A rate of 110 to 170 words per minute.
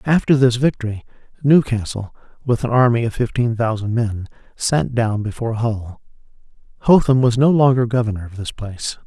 Yes: average, 150 wpm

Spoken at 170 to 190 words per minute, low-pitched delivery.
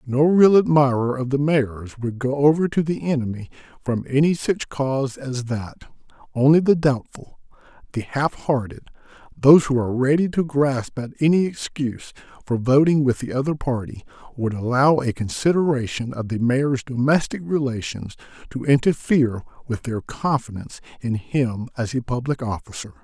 No: average, 150 wpm; low, 130 Hz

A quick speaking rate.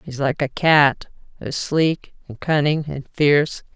No: average, 145 wpm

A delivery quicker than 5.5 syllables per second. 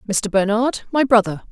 No: 5.2 syllables/s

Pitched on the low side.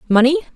No: very high, 280 Hz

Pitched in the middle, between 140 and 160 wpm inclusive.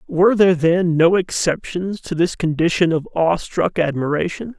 Yes: medium, 170 Hz; average, 145 wpm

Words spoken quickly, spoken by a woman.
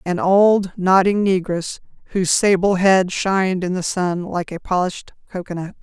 No: average, 155 wpm; female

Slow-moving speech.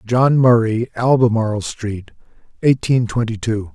Yes: slow, 110 wpm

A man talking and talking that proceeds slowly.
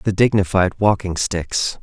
Yes: male; slow, 130 wpm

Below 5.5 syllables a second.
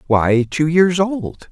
Yes: 3.0 syllables/s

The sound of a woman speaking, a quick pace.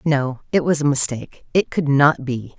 Yes: female; fast, 210 wpm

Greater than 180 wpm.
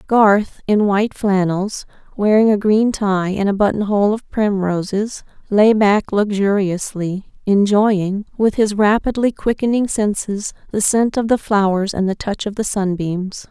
No: average, 155 wpm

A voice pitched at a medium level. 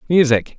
Yes: medium, 145 Hz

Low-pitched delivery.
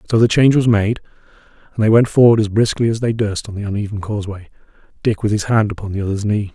Yes: low, 105 Hz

